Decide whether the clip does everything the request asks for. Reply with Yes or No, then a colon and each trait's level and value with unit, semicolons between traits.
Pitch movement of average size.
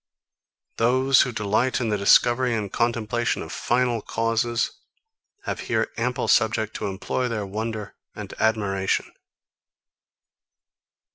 No: narrow, 2.1 semitones